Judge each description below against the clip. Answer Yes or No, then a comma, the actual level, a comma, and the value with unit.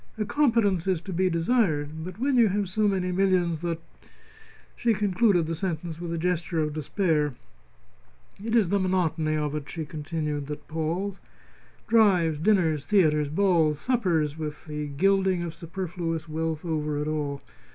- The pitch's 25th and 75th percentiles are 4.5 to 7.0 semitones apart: No, average, 3.8 semitones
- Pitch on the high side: No, medium, 170 Hz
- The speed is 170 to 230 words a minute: No, average, 160 wpm